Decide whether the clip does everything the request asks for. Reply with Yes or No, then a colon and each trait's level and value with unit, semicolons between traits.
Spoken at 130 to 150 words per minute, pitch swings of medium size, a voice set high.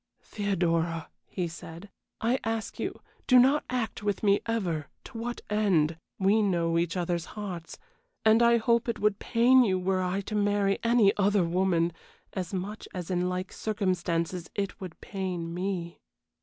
No: average, 160 wpm; average, 3.7 semitones; high, 195 Hz